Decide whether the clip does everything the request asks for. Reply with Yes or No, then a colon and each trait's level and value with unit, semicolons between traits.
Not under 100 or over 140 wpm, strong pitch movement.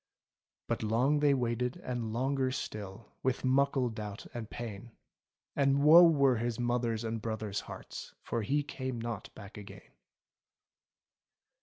No: slow, 135 wpm; average, 3.4 semitones